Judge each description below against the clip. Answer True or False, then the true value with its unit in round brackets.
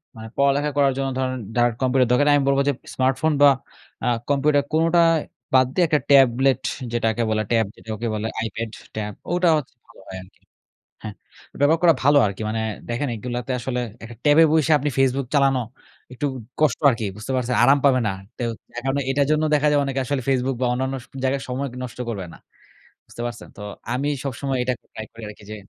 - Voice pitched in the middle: False (130 Hz)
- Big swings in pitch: False (3.2 semitones)